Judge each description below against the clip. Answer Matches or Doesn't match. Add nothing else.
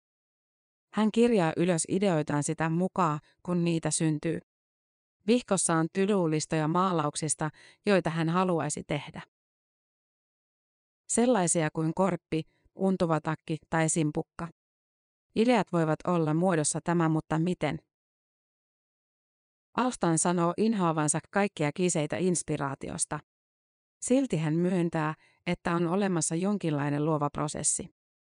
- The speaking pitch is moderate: Matches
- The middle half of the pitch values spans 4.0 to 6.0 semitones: Doesn't match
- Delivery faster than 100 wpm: Doesn't match